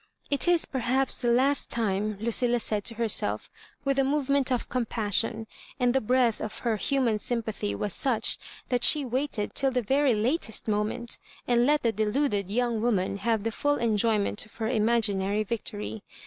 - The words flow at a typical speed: Yes, average, 175 wpm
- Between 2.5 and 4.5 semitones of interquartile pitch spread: Yes, average, 3.4 semitones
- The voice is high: Yes, high, 235 Hz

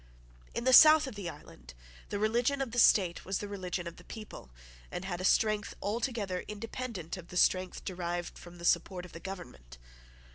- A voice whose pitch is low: No, high, 190 Hz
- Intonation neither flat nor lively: Yes, average, 4.2 semitones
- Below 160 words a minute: No, average, 190 wpm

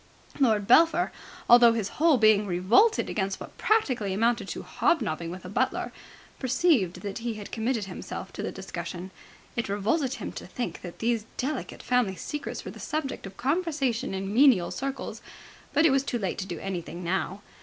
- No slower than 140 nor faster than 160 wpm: No, average, 175 wpm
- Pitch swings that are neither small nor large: No, wide, 5.8 semitones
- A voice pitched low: No, high, 225 Hz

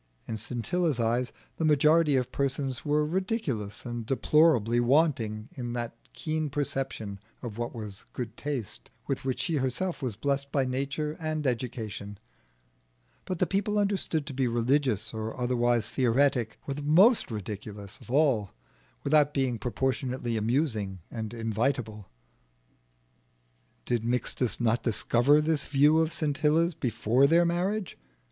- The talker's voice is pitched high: No, low, 130 Hz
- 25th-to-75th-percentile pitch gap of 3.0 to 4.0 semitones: No, average, 4.6 semitones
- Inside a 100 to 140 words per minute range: Yes, slow, 135 wpm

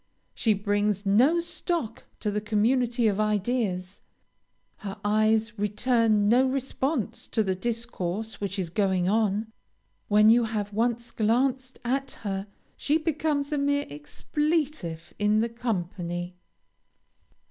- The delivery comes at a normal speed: No, slow, 125 wpm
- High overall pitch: Yes, high, 220 Hz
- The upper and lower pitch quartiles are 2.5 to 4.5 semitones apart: Yes, average, 3.8 semitones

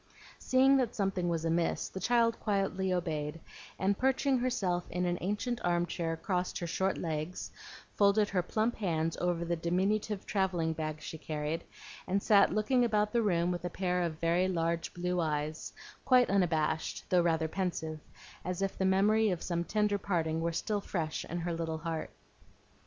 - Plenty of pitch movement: No, average, 3.5 semitones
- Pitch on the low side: No, medium, 180 Hz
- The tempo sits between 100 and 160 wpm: No, average, 175 wpm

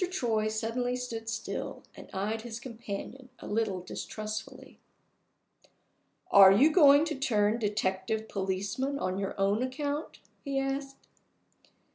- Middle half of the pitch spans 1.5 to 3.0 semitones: No, average, 4.5 semitones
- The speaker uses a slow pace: Yes, slow, 120 wpm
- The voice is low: No, high, 225 Hz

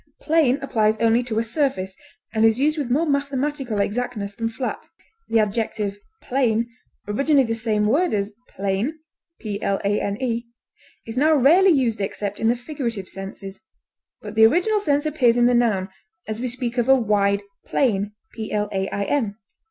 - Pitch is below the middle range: No, high, 230 Hz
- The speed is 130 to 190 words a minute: Yes, average, 145 wpm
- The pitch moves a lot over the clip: No, average, 4.5 semitones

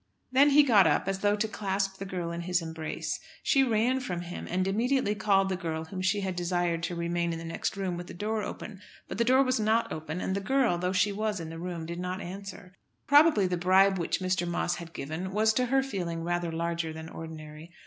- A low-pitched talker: No, medium, 185 Hz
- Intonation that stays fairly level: No, average, 3.7 semitones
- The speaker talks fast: Yes, fast, 235 wpm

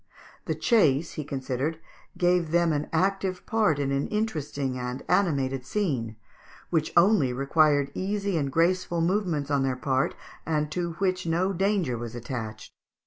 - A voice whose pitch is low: No, medium, 155 Hz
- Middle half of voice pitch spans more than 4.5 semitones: Yes, average, 5.3 semitones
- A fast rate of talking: No, average, 145 wpm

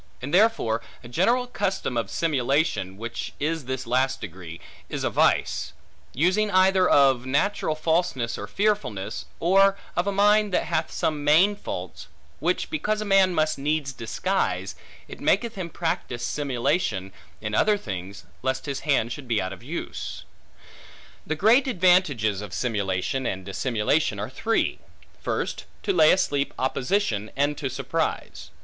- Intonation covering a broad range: Yes, wide, 8.2 semitones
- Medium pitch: Yes, medium, 145 Hz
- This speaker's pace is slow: No, average, 150 wpm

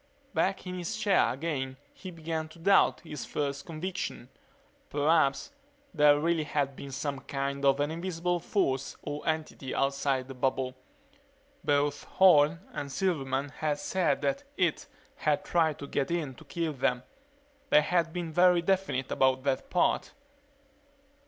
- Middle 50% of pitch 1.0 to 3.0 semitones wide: No, average, 3.7 semitones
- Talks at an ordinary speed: Yes, average, 145 wpm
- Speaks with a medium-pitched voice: Yes, medium, 150 Hz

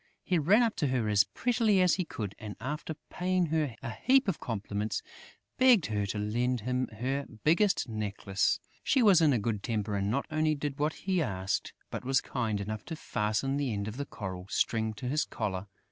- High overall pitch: No, low, 125 Hz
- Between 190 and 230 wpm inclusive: Yes, fast, 205 wpm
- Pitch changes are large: Yes, wide, 7.1 semitones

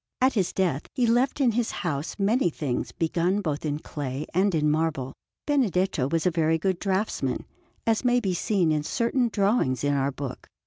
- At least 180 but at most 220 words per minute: Yes, average, 185 wpm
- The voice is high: No, medium, 180 Hz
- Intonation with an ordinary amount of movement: No, wide, 6.6 semitones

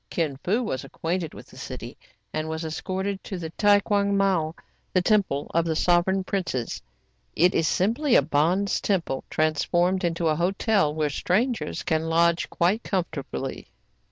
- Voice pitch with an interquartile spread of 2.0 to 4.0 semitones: Yes, average, 3.7 semitones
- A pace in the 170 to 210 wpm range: No, average, 160 wpm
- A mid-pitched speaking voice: Yes, medium, 175 Hz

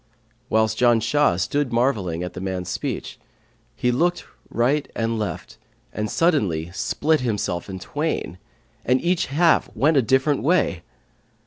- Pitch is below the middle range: Yes, low, 120 Hz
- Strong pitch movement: Yes, wide, 7.3 semitones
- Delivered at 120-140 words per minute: Yes, slow, 135 wpm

